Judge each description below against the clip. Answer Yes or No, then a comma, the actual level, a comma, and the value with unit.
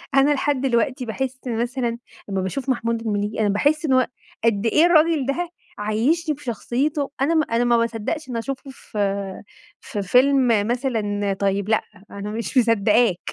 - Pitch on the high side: Yes, high, 240 Hz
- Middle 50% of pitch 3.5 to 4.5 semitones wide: Yes, average, 4.2 semitones